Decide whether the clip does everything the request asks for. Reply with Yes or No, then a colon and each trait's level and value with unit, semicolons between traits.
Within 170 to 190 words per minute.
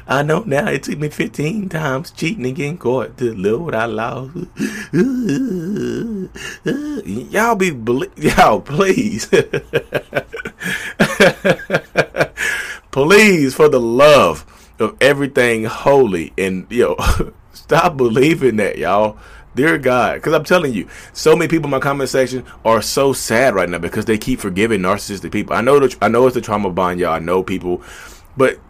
No: average, 150 wpm